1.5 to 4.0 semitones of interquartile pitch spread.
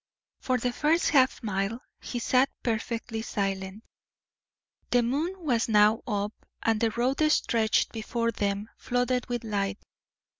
Yes: average, 2.9 semitones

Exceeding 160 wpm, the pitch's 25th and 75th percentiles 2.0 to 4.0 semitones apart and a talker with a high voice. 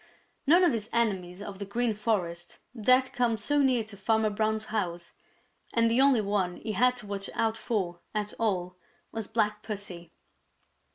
Yes: average, 170 wpm; average, 2.8 semitones; high, 215 Hz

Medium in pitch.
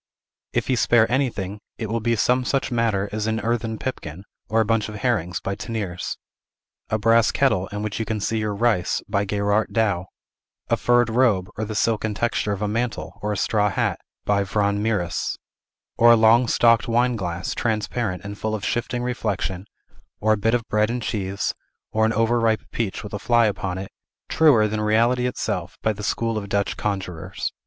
No: low, 110 Hz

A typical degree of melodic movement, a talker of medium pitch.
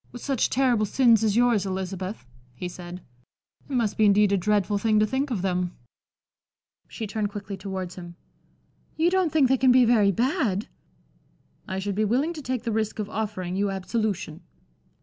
No: average, 4.2 semitones; high, 210 Hz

